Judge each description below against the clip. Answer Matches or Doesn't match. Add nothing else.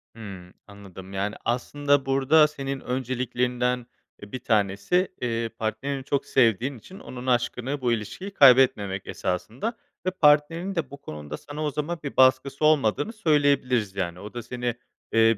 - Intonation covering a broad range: Doesn't match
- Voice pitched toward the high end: Doesn't match